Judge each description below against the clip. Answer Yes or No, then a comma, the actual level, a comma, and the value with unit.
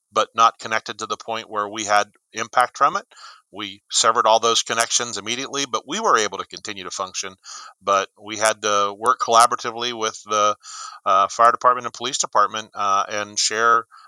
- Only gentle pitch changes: Yes, narrow, 2.0 semitones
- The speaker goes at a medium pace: Yes, average, 185 wpm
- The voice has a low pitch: Yes, low, 110 Hz